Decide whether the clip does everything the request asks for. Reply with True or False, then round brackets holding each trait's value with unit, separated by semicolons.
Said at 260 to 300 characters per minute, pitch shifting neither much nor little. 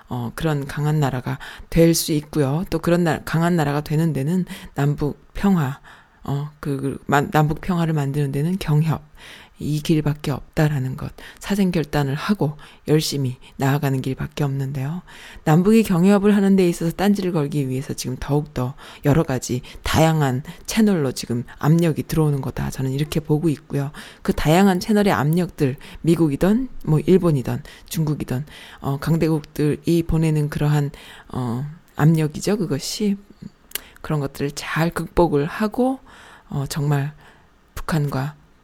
True (295 characters per minute; 3.2 semitones)